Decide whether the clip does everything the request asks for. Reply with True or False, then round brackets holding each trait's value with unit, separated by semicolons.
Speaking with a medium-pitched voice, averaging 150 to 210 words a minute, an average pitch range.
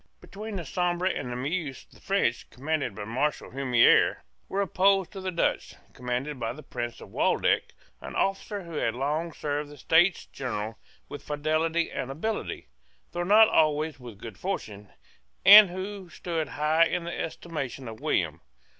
False (155 Hz; 165 wpm; 5.9 semitones)